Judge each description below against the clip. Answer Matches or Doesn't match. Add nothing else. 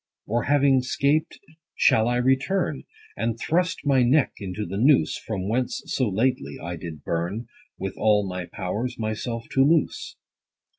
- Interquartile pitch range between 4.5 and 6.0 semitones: Matches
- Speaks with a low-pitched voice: Matches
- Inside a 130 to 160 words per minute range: Matches